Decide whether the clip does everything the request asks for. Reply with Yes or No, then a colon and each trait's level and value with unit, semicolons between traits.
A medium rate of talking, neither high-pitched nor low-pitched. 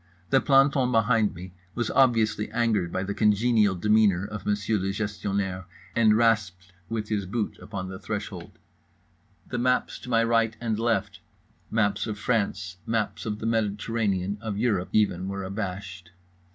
No: average, 150 wpm; low, 105 Hz